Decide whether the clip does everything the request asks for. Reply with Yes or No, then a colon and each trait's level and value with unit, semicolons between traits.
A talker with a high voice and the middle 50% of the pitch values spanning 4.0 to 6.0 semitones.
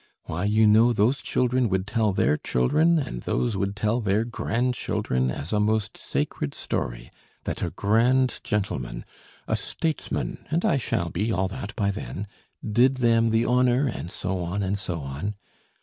No: low, 105 Hz; average, 4.4 semitones